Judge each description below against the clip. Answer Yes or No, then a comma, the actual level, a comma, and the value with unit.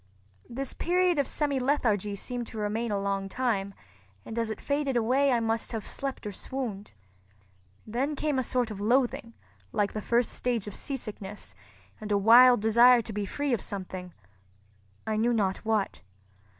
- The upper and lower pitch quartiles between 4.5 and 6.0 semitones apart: No, average, 3.9 semitones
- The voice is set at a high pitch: Yes, high, 225 Hz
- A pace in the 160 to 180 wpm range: Yes, average, 165 wpm